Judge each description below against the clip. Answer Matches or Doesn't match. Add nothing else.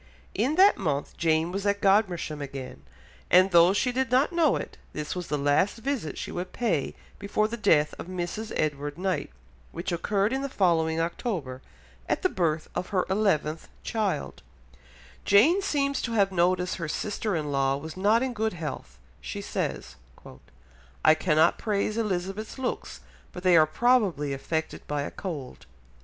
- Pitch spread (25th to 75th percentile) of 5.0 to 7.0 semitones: Matches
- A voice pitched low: Doesn't match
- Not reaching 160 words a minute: Doesn't match